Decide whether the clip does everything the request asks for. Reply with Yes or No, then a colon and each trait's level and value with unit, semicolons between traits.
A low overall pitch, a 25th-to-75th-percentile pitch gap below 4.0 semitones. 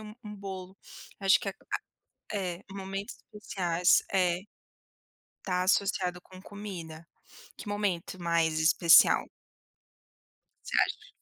No: medium, 185 Hz; narrow, 2.5 semitones